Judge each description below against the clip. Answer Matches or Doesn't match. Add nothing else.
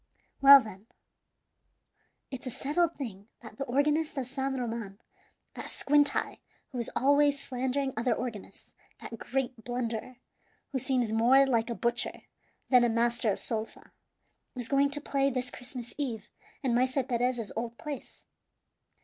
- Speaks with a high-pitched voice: Matches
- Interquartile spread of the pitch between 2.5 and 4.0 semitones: Matches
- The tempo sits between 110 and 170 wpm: Matches